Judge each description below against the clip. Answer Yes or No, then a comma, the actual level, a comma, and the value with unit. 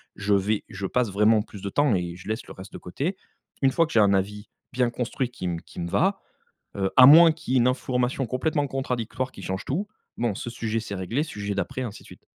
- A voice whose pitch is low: Yes, low, 115 Hz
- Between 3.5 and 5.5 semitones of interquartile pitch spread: Yes, average, 4.7 semitones